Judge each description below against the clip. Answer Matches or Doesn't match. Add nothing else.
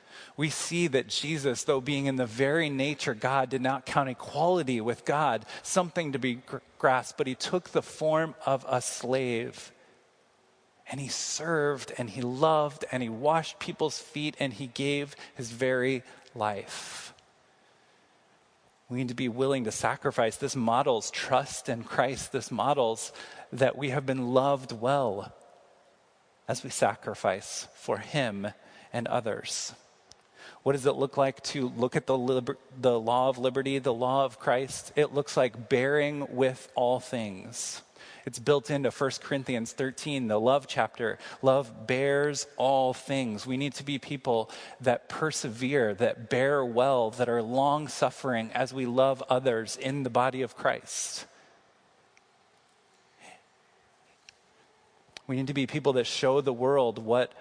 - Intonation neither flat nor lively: Doesn't match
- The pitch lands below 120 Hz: Doesn't match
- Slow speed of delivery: Doesn't match